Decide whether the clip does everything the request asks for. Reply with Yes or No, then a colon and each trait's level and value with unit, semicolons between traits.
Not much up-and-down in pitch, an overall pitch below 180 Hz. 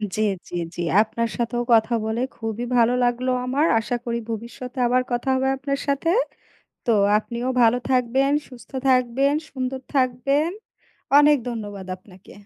No: narrow, 2.3 semitones; high, 245 Hz